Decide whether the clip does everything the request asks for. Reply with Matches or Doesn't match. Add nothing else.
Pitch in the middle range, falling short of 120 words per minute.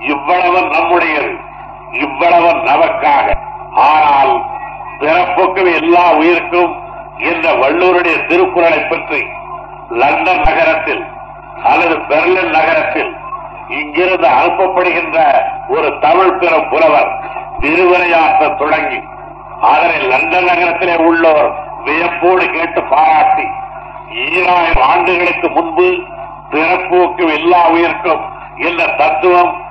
Matches